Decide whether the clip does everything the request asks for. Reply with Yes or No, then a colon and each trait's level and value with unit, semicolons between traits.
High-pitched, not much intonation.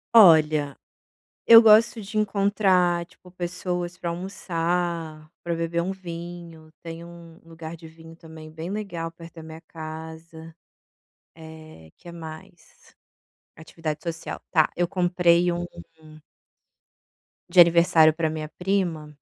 No: medium, 170 Hz; narrow, 1.8 semitones